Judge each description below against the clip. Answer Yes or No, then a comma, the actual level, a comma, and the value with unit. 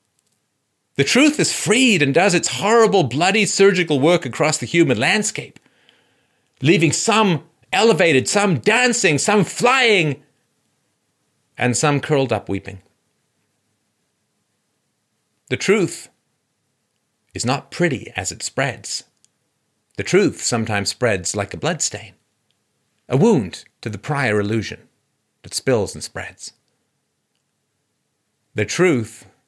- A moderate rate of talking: No, slow, 110 wpm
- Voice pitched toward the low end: No, medium, 145 Hz